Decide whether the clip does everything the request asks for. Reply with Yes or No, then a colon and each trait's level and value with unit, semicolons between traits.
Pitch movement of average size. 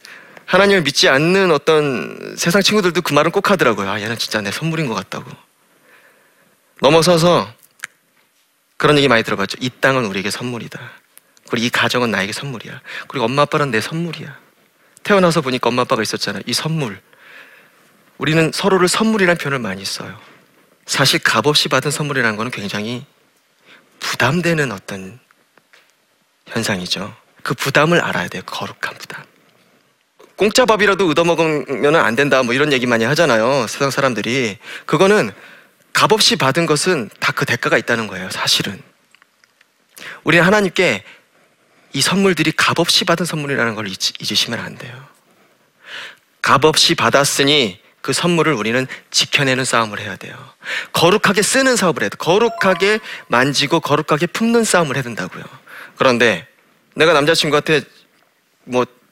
No: wide, 6.3 semitones